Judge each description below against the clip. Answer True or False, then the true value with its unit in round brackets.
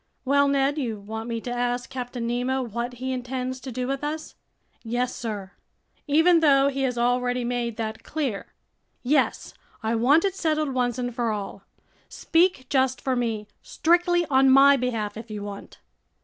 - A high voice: True (250 Hz)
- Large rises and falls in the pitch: False (2.7 semitones)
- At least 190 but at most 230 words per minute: False (170 wpm)